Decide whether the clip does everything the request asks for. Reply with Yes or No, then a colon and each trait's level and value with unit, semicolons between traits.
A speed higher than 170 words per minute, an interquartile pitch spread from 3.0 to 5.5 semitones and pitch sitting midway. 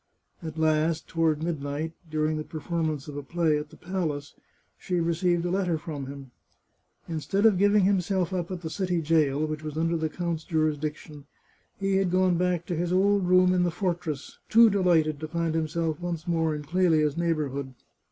No: average, 190 wpm; narrow, 2.6 semitones; medium, 165 Hz